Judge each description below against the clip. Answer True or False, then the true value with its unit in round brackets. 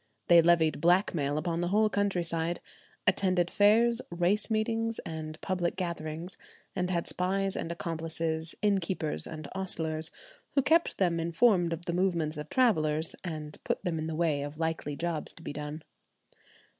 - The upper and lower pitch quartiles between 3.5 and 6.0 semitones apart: False (3.0 semitones)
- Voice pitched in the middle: True (170 Hz)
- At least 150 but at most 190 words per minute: True (155 wpm)